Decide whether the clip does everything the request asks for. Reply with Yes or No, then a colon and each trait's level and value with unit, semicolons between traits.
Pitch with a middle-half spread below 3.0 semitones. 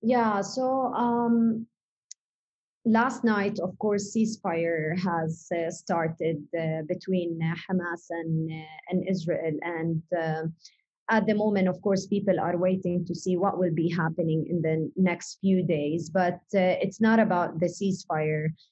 No: average, 3.4 semitones